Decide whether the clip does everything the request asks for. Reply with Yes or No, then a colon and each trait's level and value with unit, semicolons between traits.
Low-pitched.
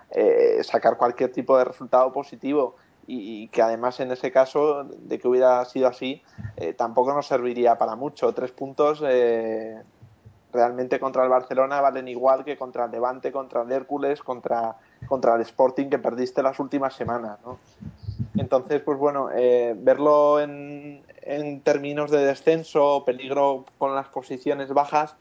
Yes: low, 130 Hz